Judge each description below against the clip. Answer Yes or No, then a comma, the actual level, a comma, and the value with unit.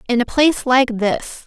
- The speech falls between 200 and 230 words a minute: Yes, fast, 205 wpm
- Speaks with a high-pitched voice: Yes, very high, 250 Hz